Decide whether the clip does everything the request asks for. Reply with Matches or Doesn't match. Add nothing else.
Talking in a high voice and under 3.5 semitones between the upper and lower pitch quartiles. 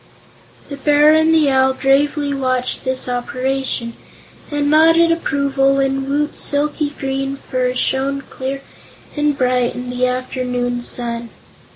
Matches